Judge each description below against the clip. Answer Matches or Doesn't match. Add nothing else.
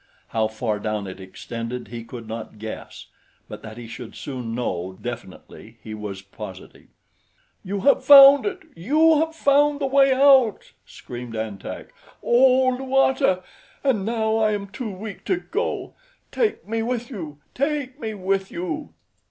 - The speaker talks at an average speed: Matches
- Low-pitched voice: Doesn't match